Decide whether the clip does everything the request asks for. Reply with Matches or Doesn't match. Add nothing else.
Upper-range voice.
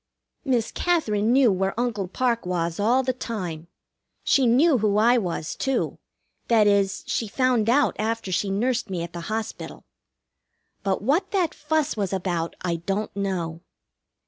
Matches